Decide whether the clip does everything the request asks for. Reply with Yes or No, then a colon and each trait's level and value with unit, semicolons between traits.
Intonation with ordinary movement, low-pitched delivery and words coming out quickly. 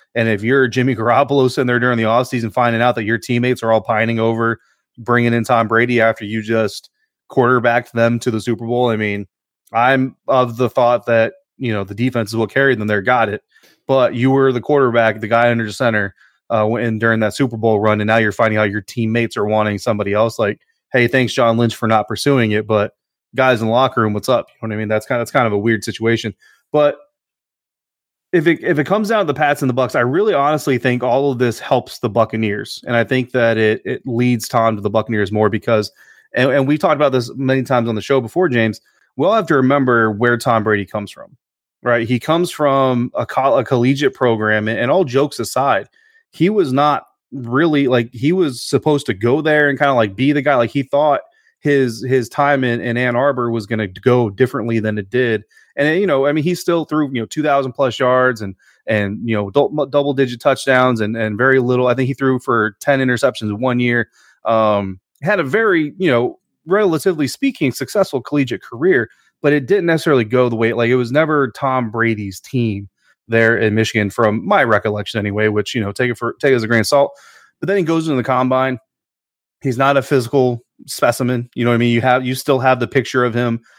Yes: average, 3.3 semitones; low, 120 Hz; fast, 230 wpm